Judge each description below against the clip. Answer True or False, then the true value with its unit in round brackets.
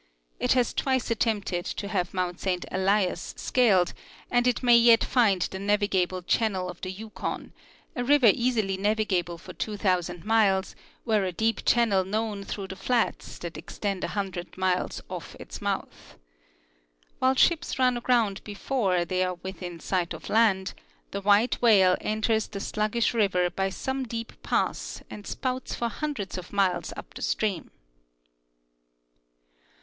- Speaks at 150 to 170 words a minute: True (155 wpm)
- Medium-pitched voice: False (205 Hz)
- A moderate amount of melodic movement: True (3.7 semitones)